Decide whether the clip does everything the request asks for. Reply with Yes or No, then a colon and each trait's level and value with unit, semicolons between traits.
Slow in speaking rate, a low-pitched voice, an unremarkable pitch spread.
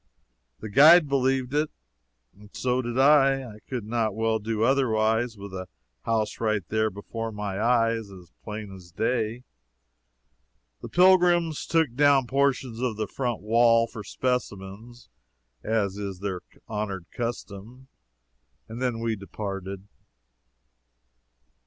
Yes: slow, 125 wpm; low, 115 Hz; average, 3.6 semitones